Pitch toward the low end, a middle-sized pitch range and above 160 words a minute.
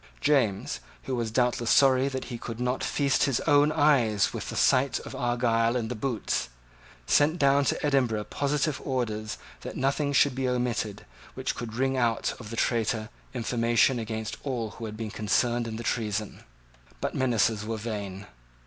Yes: low, 120 Hz; average, 3.3 semitones; average, 170 wpm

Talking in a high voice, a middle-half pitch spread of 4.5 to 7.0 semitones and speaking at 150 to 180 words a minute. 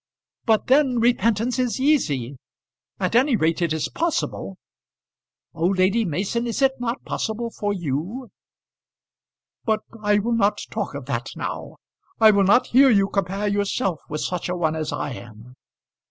Yes: high, 205 Hz; wide, 5.5 semitones; average, 155 wpm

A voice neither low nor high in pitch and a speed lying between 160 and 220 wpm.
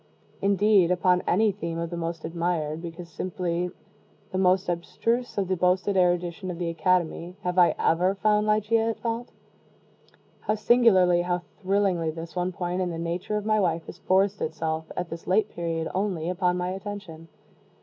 Yes: medium, 180 Hz; average, 170 wpm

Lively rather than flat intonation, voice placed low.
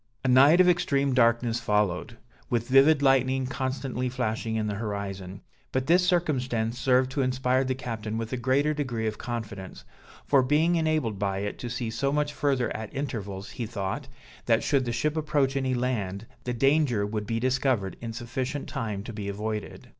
No: average, 3.7 semitones; low, 125 Hz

